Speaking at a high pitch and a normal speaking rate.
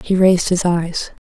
No: medium, 180 Hz; average, 190 wpm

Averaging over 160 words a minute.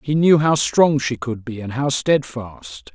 Yes: fast, 205 wpm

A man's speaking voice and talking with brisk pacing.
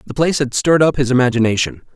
Yes: male; fast, 215 wpm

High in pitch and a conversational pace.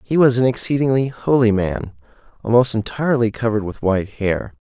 No: low, 115 Hz; average, 155 wpm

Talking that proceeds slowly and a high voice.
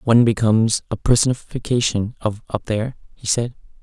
No: slow, 125 wpm; low, 115 Hz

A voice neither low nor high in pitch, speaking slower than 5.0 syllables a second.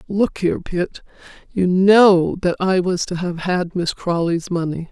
Yes: medium, 180 Hz; 4.1 syllables/s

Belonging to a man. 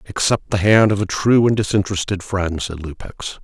Yes: male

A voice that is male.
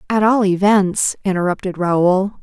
No: female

